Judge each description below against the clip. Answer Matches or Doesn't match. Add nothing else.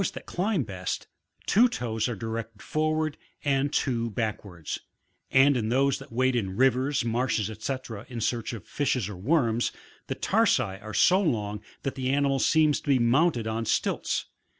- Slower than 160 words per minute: Doesn't match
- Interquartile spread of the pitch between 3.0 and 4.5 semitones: Matches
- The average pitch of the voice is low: Matches